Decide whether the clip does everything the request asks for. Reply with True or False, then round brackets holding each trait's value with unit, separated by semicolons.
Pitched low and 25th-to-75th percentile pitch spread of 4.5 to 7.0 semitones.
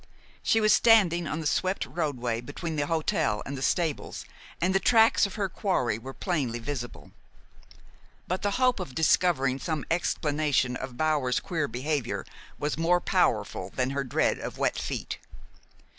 False (155 Hz; 5.3 semitones)